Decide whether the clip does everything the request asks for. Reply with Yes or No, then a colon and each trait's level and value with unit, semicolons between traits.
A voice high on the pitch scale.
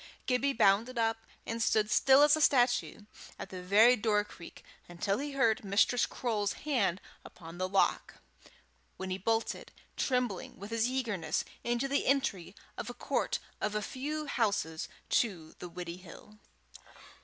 Yes: high, 220 Hz